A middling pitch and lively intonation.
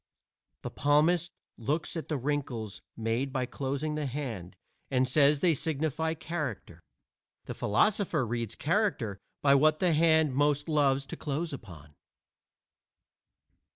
No: medium, 145 Hz; average, 4.0 semitones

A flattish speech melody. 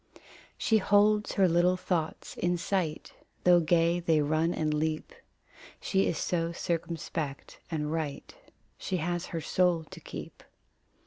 Yes: narrow, 2.3 semitones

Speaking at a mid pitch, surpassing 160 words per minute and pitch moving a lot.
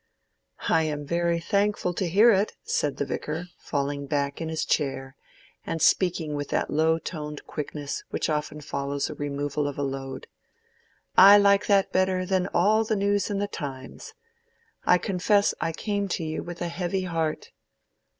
No: medium, 165 Hz; average, 170 wpm; average, 4.7 semitones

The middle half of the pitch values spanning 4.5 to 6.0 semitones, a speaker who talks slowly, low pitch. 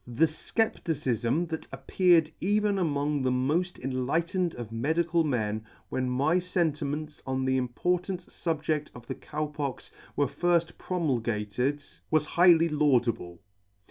No: average, 4.8 semitones; slow, 125 wpm; medium, 150 Hz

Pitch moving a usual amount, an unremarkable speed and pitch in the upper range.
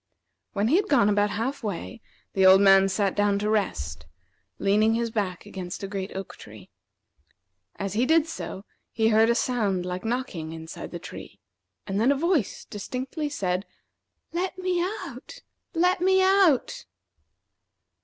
No: wide, 6.2 semitones; average, 155 wpm; high, 210 Hz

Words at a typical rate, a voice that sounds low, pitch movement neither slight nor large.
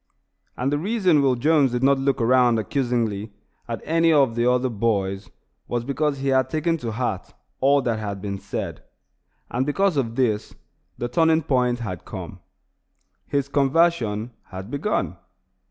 Yes: average, 155 wpm; low, 130 Hz; average, 4.0 semitones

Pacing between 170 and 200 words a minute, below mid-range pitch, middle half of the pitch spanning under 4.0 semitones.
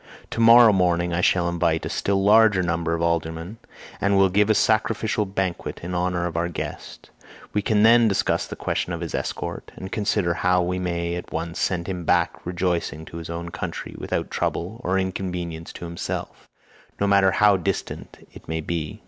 Yes: average, 190 wpm; very low, 90 Hz; average, 2.7 semitones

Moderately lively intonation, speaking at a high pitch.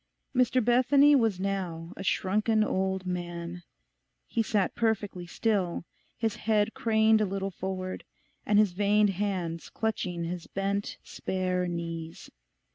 Yes: average, 3.4 semitones; high, 195 Hz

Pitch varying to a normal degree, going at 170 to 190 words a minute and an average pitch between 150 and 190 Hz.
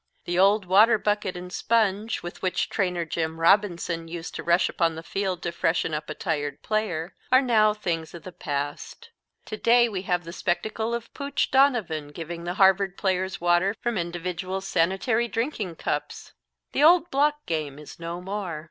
Yes: average, 4.2 semitones; average, 175 wpm; medium, 185 Hz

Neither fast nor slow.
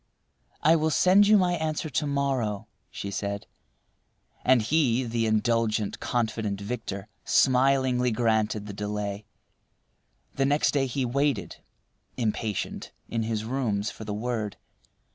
No: slow, 125 wpm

